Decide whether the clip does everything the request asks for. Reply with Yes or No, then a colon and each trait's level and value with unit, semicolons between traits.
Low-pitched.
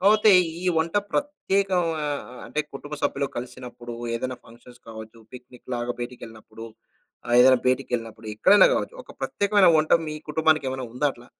Yes: low, 130 Hz